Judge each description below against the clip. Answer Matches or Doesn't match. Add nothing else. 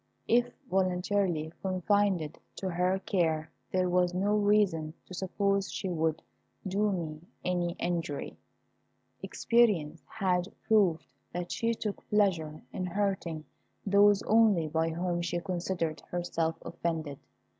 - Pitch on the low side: Doesn't match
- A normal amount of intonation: Matches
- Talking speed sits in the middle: Doesn't match